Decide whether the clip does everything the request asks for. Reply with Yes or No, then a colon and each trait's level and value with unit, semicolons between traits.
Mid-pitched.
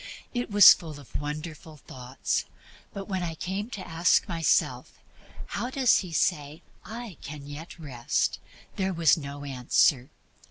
Yes: medium, 160 Hz